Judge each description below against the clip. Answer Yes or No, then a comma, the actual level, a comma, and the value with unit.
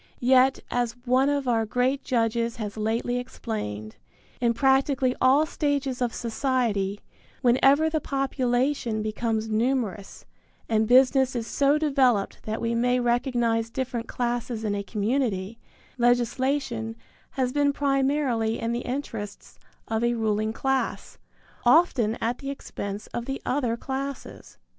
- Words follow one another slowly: Yes, slow, 130 wpm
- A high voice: Yes, high, 245 Hz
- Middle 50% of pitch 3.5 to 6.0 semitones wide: No, average, 3.0 semitones